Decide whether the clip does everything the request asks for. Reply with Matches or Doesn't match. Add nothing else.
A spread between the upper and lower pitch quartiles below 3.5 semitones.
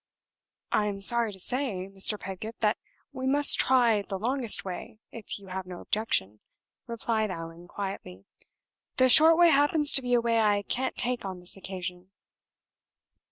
Doesn't match